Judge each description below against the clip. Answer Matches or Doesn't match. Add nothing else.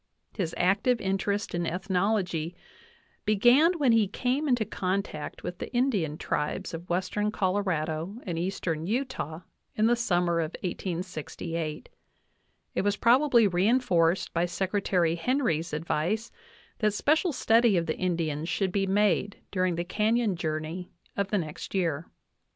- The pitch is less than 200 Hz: Matches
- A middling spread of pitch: Matches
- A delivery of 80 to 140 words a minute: Matches